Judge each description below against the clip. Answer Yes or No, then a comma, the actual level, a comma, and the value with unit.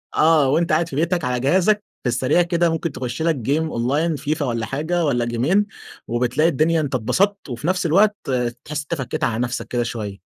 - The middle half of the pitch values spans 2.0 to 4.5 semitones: No, average, 5.2 semitones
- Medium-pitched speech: Yes, medium, 150 Hz